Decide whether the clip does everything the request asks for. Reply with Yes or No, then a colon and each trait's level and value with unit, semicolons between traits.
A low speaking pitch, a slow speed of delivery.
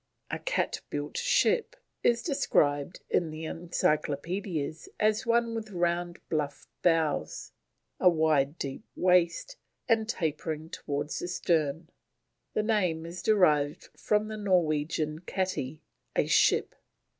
No: medium, 170 Hz; slow, 120 wpm